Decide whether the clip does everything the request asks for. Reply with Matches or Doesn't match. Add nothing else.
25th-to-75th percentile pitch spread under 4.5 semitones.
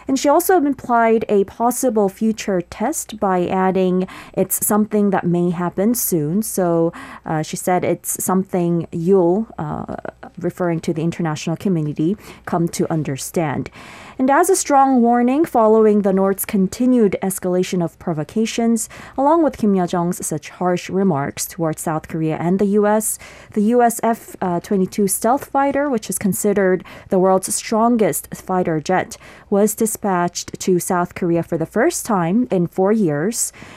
Matches